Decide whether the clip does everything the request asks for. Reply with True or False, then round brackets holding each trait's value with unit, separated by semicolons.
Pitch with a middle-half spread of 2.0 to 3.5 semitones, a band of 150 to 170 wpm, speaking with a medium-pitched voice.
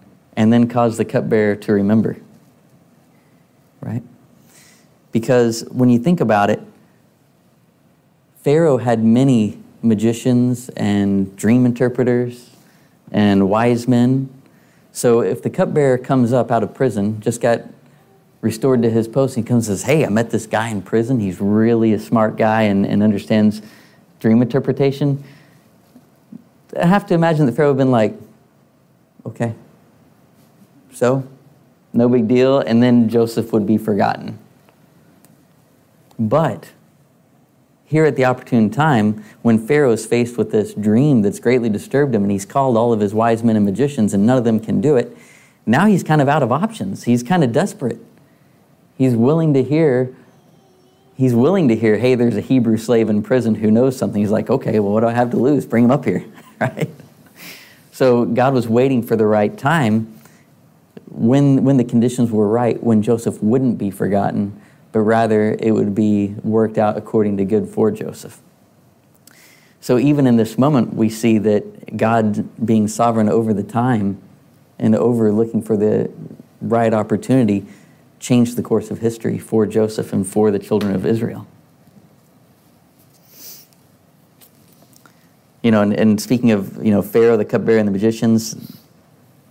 False (3.0 semitones; 160 wpm; 115 Hz)